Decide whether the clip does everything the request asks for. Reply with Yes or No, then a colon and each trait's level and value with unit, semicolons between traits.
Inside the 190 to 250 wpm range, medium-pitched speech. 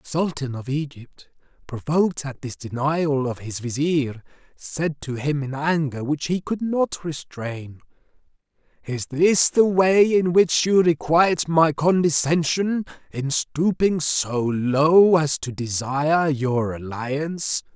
No: slow, 135 wpm; medium, 150 Hz